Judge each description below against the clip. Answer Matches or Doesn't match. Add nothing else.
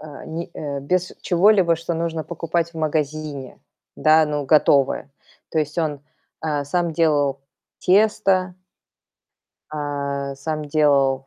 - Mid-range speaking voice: Matches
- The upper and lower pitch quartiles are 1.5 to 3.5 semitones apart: Matches